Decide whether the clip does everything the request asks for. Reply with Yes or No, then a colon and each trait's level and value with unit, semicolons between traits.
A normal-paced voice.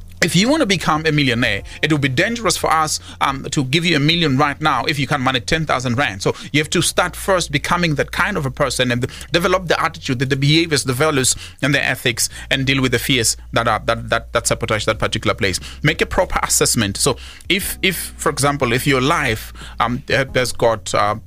No: fast, 230 wpm